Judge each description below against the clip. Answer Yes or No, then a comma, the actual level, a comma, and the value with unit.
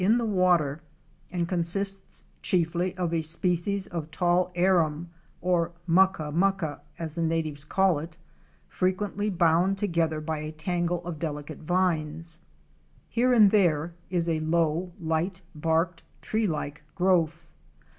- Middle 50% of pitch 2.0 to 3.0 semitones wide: Yes, narrow, 2.6 semitones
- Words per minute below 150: Yes, slow, 135 wpm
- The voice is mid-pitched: Yes, medium, 170 Hz